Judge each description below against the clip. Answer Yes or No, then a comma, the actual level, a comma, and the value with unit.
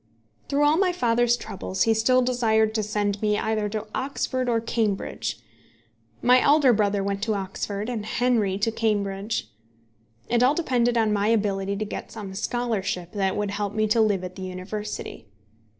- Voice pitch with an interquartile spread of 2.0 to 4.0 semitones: Yes, average, 3.0 semitones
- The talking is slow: No, average, 170 wpm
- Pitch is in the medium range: No, high, 215 Hz